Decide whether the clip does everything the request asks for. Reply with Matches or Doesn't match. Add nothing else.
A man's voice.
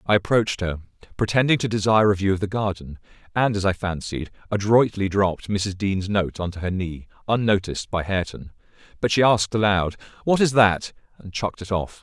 Matches